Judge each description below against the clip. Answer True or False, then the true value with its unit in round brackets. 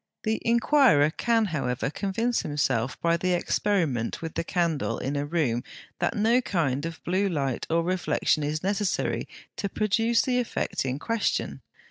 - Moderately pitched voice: True (170 Hz)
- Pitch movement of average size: False (6.7 semitones)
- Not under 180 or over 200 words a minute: False (155 wpm)